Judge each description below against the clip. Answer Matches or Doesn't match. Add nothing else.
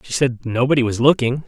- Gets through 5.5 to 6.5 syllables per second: Matches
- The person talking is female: Doesn't match